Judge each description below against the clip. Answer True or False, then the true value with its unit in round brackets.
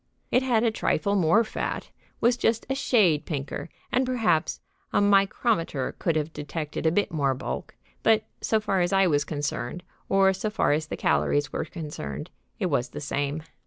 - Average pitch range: False (6.5 semitones)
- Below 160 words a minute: False (180 wpm)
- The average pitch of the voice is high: False (175 Hz)